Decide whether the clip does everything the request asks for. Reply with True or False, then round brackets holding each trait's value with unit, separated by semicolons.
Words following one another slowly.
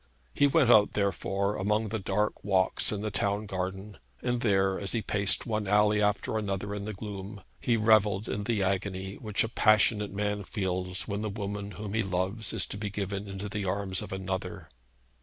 False (195 wpm)